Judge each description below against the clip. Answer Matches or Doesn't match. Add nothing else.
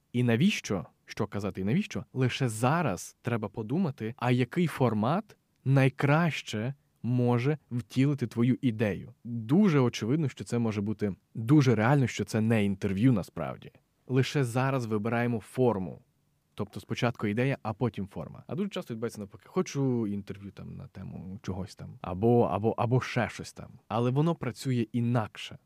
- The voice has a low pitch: Matches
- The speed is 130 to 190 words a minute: Matches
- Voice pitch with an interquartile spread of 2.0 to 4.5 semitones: Matches